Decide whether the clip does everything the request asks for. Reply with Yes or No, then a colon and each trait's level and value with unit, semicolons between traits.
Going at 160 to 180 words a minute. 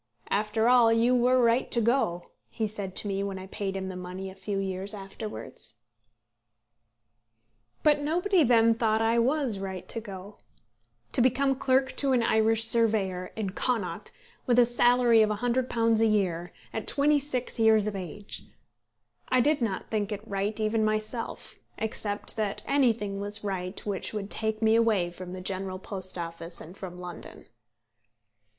Yes: average, 165 wpm